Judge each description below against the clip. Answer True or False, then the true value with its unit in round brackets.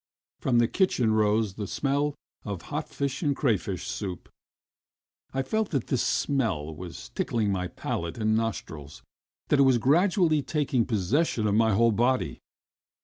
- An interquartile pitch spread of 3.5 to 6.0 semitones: True (5.6 semitones)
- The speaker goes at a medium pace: True (150 wpm)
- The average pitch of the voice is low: True (115 Hz)